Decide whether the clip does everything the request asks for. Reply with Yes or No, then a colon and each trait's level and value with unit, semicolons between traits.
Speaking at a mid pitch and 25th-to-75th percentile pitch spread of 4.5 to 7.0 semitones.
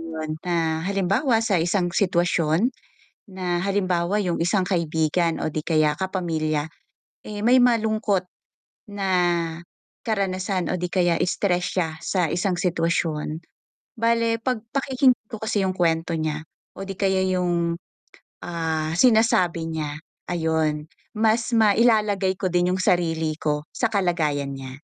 No: medium, 180 Hz; average, 3.8 semitones